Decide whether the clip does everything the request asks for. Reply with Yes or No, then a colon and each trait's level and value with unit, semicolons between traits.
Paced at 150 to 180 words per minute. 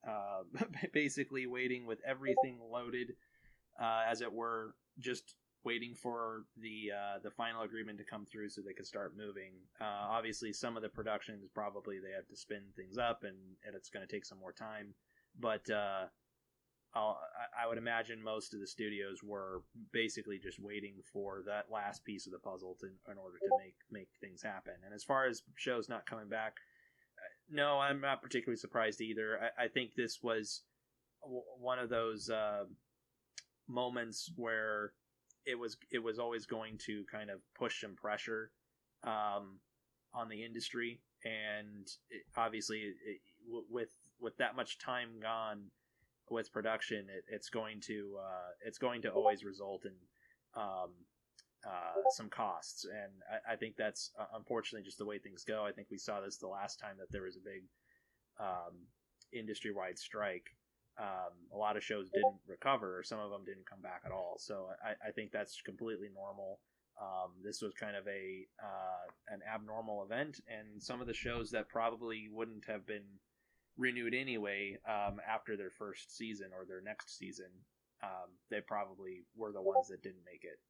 Yes: average, 175 wpm